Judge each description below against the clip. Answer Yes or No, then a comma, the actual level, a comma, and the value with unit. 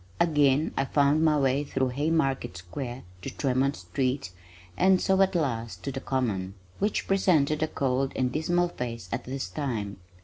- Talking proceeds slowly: No, average, 165 wpm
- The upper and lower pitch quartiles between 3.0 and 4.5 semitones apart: Yes, average, 3.6 semitones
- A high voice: No, low, 135 Hz